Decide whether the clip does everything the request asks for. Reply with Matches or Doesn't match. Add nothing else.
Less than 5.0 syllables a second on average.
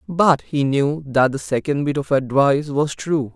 Matches